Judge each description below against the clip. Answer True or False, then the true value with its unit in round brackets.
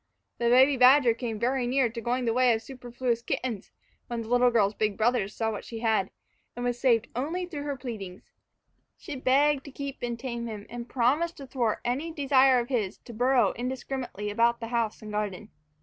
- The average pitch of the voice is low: False (240 Hz)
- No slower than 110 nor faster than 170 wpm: False (200 wpm)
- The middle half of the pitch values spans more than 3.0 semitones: False (2.5 semitones)